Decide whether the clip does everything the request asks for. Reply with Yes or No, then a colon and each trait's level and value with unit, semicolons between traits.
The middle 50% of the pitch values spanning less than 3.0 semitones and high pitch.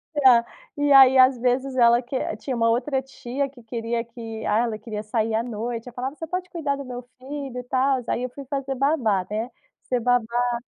Yes: narrow, 2.6 semitones; high, 245 Hz